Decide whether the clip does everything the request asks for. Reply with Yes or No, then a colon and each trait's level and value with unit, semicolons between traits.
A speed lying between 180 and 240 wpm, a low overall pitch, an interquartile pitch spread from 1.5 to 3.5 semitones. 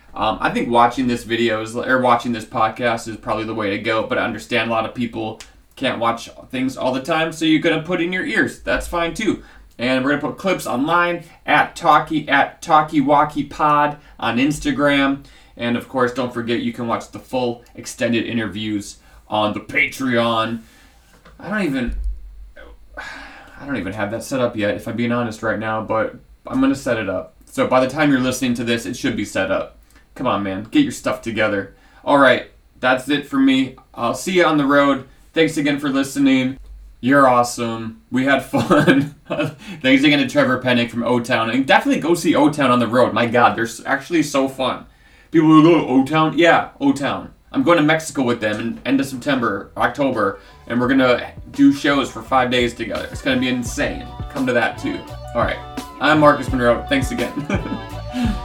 No: fast, 205 wpm; low, 130 Hz; average, 4.9 semitones